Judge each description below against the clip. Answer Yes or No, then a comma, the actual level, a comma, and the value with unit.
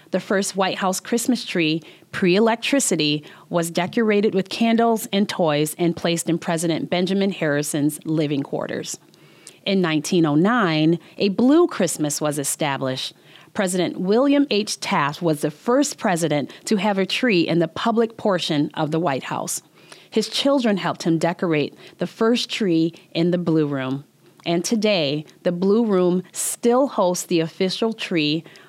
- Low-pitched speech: No, medium, 180 Hz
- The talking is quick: No, average, 150 wpm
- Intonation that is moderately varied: Yes, average, 4.7 semitones